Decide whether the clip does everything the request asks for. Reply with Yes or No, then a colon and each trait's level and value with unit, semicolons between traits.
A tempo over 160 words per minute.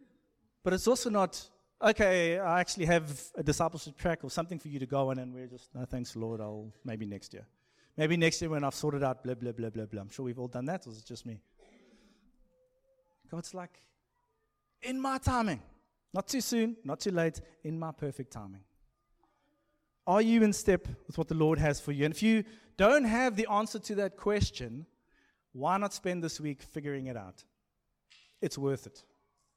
Yes: average, 200 wpm